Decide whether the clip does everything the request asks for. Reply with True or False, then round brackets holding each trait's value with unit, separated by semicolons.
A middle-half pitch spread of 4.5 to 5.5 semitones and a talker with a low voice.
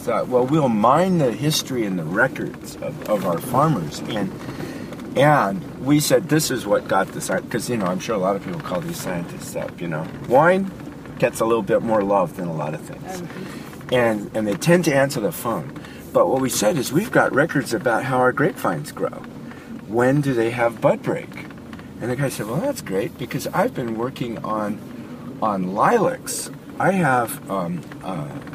True (5.0 semitones; 130 Hz)